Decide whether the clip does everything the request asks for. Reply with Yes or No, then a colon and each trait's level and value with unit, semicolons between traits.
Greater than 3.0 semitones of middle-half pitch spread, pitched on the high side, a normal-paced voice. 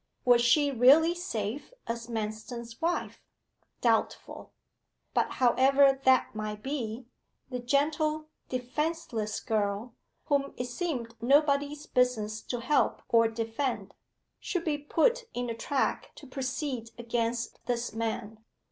No: average, 3.9 semitones; very high, 250 Hz; slow, 120 wpm